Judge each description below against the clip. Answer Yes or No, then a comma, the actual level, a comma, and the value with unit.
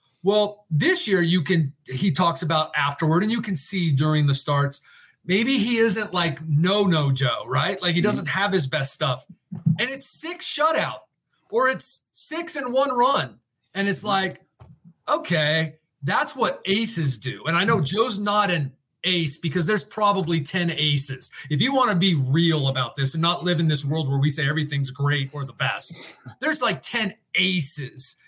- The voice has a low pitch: No, medium, 170 Hz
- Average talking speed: Yes, average, 185 wpm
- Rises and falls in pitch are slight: No, wide, 5.5 semitones